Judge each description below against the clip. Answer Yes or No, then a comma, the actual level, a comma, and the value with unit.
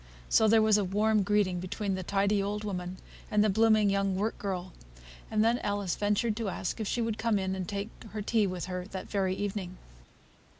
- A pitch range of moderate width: No, narrow, 2.2 semitones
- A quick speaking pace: Yes, fast, 210 wpm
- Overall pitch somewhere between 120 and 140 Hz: No, high, 205 Hz